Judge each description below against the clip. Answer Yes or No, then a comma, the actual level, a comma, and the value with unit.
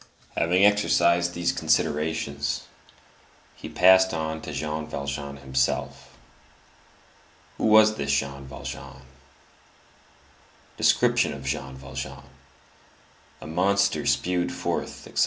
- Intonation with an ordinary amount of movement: Yes, average, 4.2 semitones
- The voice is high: No, very low, 75 Hz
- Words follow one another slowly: Yes, slow, 100 wpm